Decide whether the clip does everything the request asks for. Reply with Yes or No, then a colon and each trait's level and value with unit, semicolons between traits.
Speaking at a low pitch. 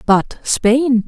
No: high, 240 Hz